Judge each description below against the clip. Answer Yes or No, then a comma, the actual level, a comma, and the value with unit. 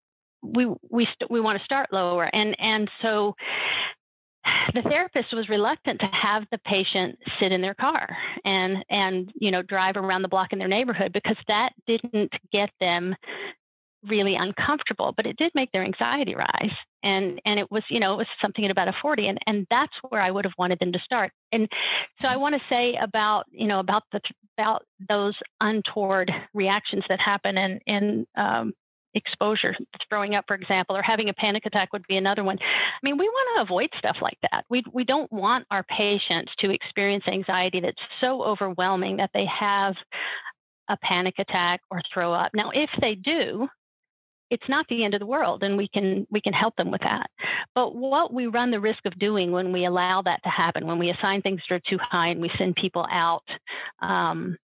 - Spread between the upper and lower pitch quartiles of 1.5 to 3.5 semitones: Yes, average, 2.9 semitones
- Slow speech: No, average, 200 wpm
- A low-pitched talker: No, high, 205 Hz